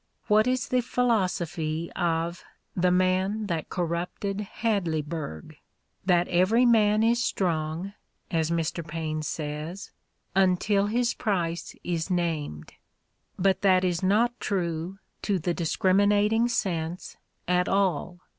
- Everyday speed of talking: No, slow, 115 wpm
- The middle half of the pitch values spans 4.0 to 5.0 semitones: No, average, 3.6 semitones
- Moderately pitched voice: Yes, medium, 180 Hz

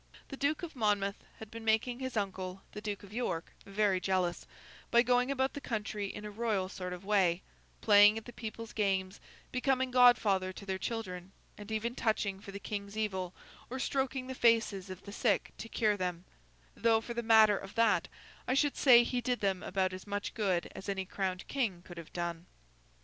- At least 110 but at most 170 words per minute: No, average, 195 wpm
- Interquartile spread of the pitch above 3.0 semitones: Yes, average, 3.8 semitones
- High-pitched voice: Yes, high, 210 Hz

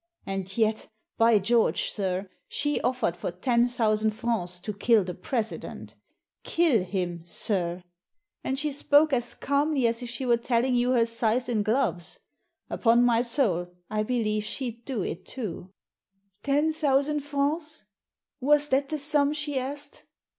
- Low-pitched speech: No, high, 235 Hz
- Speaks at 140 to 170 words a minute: Yes, average, 160 wpm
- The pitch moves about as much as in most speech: Yes, average, 4.8 semitones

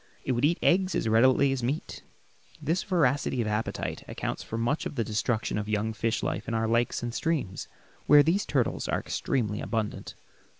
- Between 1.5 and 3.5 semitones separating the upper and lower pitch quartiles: No, average, 4.6 semitones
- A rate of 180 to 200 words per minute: Yes, average, 185 wpm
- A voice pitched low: Yes, low, 120 Hz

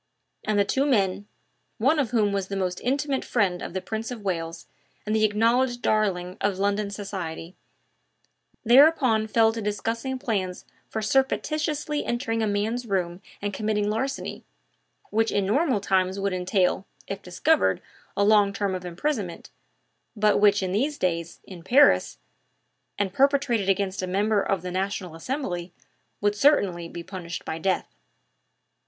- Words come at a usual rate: Yes, average, 150 wpm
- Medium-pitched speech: No, high, 205 Hz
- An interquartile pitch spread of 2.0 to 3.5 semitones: No, average, 3.9 semitones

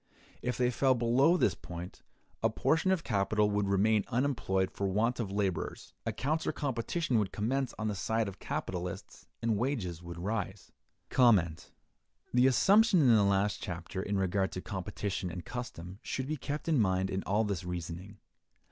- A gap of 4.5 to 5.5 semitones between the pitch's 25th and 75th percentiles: Yes, average, 4.8 semitones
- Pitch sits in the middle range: No, low, 105 Hz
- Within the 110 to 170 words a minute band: Yes, average, 165 wpm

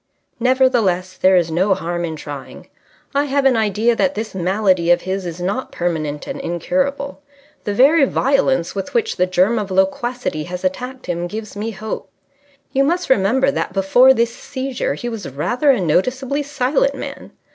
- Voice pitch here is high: Yes, high, 215 Hz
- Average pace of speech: Yes, average, 170 wpm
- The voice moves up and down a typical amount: No, wide, 6.4 semitones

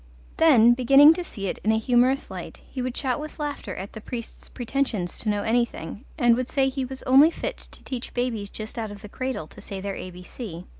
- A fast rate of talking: Yes, fast, 220 wpm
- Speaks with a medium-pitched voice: No, high, 240 Hz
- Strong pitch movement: No, average, 4.1 semitones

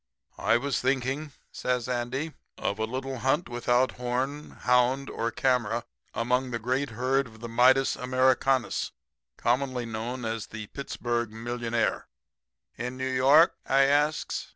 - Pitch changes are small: Yes, narrow, 2.0 semitones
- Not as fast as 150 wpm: Yes, slow, 135 wpm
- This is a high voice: No, low, 125 Hz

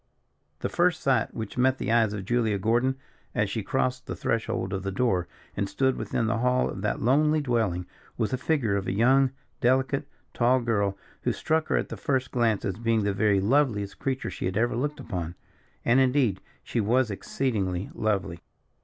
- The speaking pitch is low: Yes, low, 115 Hz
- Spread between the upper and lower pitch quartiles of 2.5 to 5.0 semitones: Yes, average, 4.5 semitones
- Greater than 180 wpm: Yes, average, 190 wpm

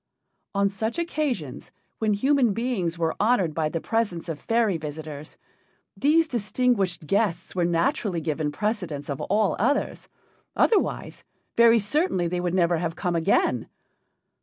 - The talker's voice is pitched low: No, high, 190 Hz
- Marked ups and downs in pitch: Yes, wide, 5.8 semitones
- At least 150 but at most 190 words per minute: No, slow, 135 wpm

